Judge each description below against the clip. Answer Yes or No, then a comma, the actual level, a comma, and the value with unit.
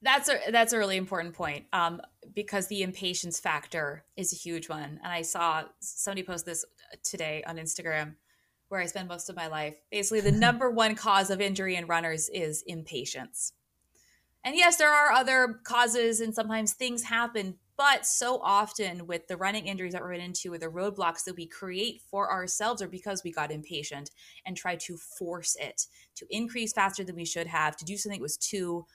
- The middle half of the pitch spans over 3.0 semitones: Yes, average, 4.1 semitones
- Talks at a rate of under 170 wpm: No, average, 195 wpm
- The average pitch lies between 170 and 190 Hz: Yes, medium, 185 Hz